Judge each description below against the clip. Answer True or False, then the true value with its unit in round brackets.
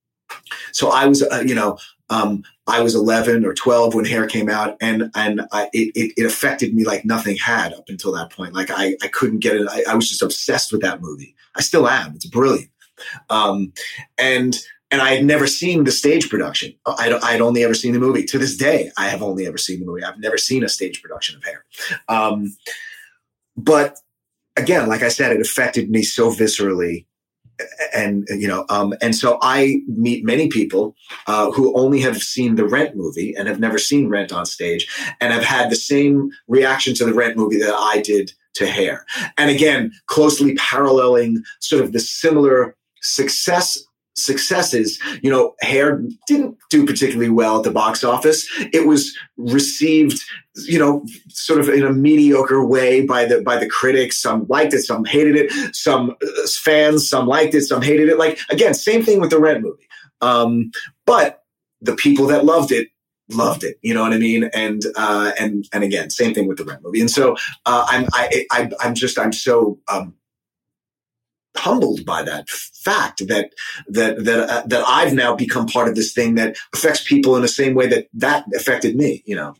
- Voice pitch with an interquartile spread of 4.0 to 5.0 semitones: True (4.7 semitones)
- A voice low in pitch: True (125 Hz)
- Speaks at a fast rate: False (195 wpm)